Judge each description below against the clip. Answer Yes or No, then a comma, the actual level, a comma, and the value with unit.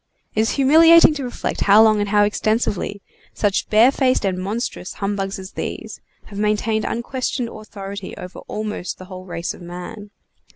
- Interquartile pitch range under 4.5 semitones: Yes, average, 2.8 semitones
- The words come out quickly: No, average, 160 wpm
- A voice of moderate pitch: No, high, 210 Hz